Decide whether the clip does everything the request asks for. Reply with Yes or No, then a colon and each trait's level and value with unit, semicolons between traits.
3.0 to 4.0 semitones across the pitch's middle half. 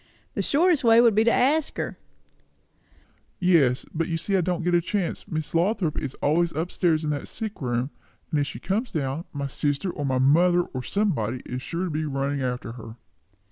No: average, 5.3 semitones